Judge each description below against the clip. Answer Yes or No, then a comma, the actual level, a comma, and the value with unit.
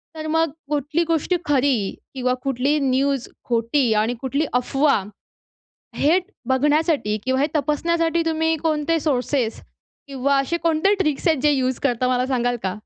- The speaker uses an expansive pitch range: No, average, 3.7 semitones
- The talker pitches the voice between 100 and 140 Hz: No, very high, 280 Hz